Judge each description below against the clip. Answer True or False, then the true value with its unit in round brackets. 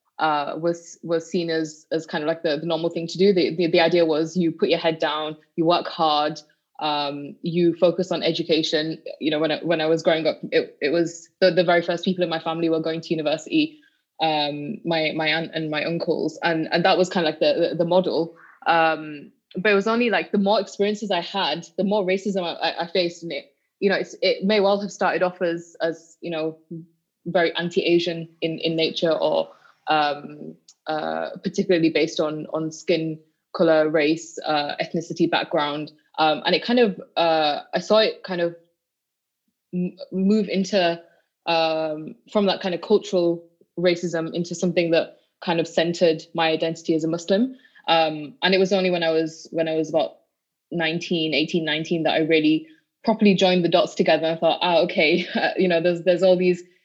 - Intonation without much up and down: True (2.2 semitones)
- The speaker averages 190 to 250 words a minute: True (200 wpm)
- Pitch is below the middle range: False (170 Hz)